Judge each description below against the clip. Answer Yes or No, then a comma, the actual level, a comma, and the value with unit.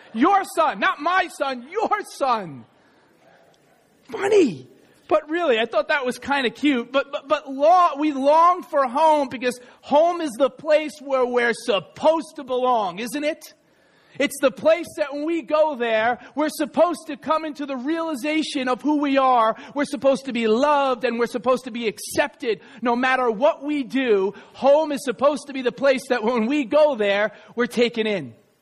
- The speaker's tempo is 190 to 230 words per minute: No, average, 180 wpm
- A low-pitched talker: No, very high, 280 Hz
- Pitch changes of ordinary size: Yes, average, 3.9 semitones